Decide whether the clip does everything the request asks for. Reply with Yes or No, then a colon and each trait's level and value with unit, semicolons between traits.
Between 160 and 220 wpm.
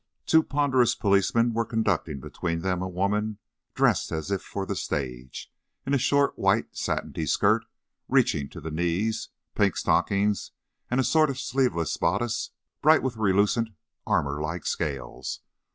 No: average, 150 wpm